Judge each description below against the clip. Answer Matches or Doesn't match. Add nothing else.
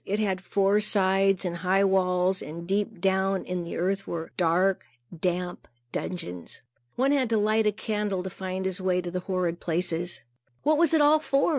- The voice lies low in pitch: Doesn't match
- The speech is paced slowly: Doesn't match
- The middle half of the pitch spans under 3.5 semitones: Matches